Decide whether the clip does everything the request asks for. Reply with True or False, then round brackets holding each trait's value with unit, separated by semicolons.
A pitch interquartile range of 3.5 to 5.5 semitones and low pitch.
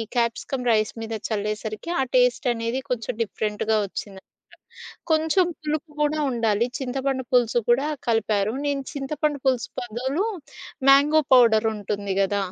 False (4.1 semitones; 240 Hz)